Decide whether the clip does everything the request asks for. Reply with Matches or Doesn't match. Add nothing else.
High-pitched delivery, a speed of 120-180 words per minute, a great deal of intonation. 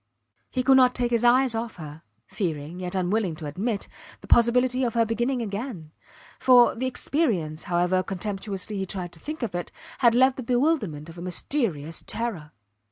Matches